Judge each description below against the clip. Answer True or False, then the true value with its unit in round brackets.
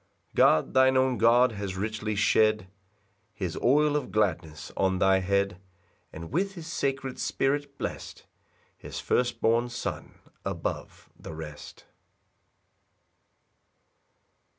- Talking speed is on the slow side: True (115 wpm)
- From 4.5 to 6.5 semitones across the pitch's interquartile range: True (5.6 semitones)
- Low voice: True (110 Hz)